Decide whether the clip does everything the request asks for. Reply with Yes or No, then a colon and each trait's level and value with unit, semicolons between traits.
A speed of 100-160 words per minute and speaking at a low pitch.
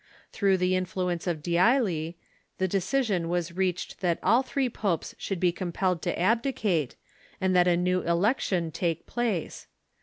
No: average, 155 wpm; medium, 185 Hz